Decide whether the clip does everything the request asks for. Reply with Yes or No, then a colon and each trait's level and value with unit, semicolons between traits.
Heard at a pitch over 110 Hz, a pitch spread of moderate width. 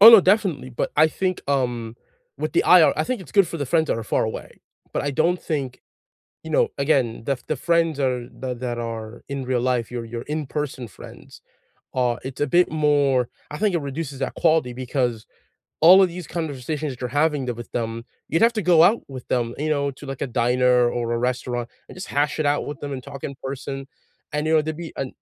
Yes: medium, 140 Hz; average, 4.1 semitones